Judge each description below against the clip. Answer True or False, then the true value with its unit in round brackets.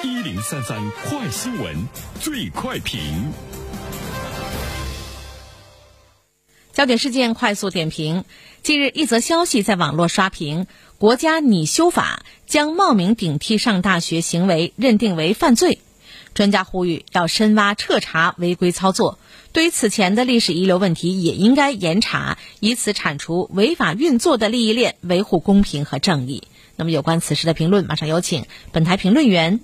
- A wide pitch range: True (5.7 semitones)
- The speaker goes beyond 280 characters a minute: False (235 characters per minute)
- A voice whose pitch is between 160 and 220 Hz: True (185 Hz)